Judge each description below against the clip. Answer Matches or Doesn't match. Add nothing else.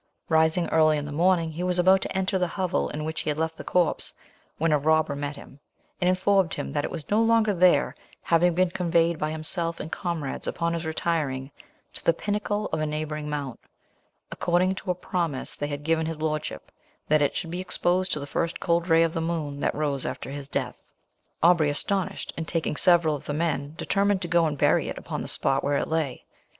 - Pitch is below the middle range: Doesn't match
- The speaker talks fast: Matches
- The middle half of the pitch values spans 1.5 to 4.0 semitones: Matches